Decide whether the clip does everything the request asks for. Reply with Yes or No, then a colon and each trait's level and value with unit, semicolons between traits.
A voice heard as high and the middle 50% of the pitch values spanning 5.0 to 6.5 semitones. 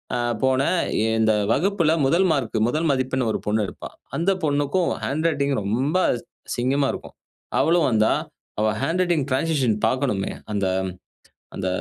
No: medium, 140 Hz; wide, 5.4 semitones